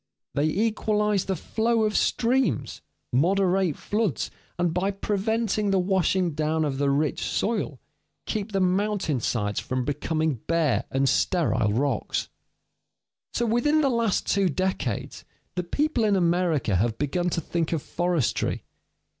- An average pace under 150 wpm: Yes, average, 140 wpm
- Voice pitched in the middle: Yes, medium, 180 Hz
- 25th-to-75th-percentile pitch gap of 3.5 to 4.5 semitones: No, wide, 5.6 semitones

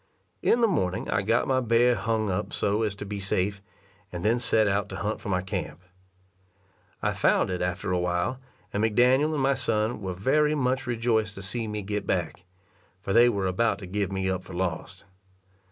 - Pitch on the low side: Yes, low, 105 Hz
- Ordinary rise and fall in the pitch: Yes, average, 3.9 semitones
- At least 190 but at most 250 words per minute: Yes, average, 200 wpm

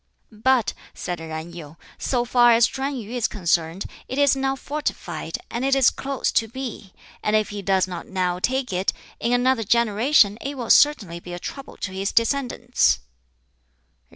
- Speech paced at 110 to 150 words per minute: No, average, 175 wpm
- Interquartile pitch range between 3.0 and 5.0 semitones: No, wide, 5.6 semitones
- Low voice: No, high, 230 Hz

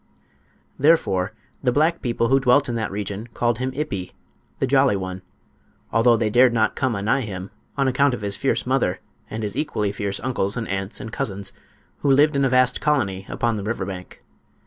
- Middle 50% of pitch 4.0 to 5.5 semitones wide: Yes, average, 4.8 semitones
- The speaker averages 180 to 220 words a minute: Yes, average, 190 wpm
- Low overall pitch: Yes, low, 115 Hz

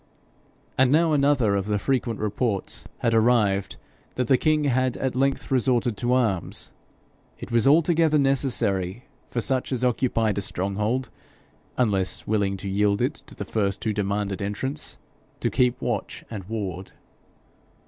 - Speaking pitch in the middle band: No, low, 115 Hz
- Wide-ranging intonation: No, average, 4.5 semitones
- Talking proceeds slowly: No, average, 150 wpm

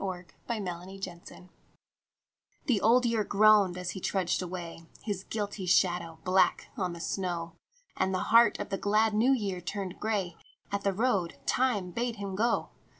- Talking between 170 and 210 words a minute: No, average, 155 wpm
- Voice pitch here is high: Yes, high, 195 Hz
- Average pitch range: Yes, average, 3.0 semitones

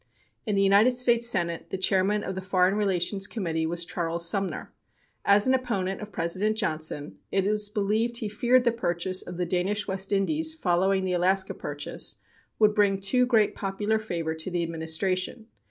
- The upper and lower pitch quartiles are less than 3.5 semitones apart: Yes, average, 3.1 semitones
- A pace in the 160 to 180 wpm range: Yes, average, 175 wpm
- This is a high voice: Yes, high, 195 Hz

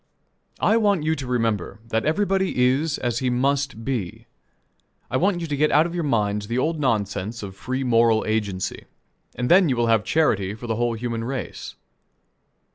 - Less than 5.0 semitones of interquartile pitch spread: No, average, 5.3 semitones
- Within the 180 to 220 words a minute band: Yes, average, 185 wpm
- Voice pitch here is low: Yes, low, 125 Hz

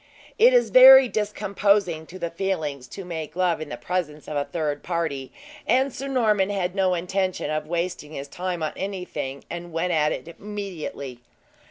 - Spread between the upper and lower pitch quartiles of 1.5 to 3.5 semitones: No, average, 4.2 semitones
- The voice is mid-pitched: Yes, medium, 180 Hz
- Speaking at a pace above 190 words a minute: No, average, 175 wpm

